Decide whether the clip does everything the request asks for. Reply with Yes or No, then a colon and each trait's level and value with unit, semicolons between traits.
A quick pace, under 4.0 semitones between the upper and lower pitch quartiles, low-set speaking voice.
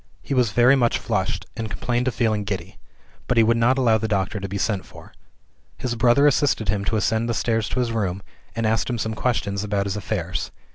Yes: fast, 225 wpm; average, 3.0 semitones; low, 110 Hz